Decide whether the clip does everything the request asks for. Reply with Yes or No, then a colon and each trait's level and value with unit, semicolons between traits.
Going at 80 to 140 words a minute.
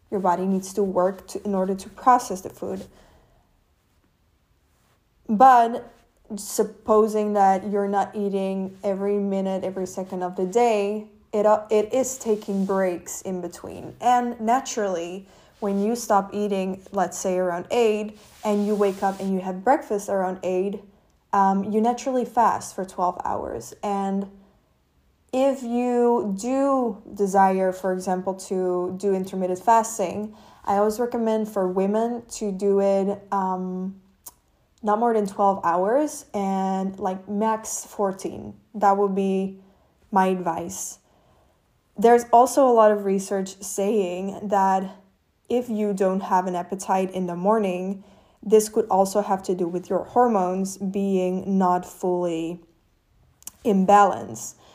Yes: slow, 135 wpm